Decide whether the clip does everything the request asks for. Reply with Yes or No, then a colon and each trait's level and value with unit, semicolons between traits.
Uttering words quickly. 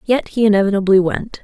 No: average, 170 wpm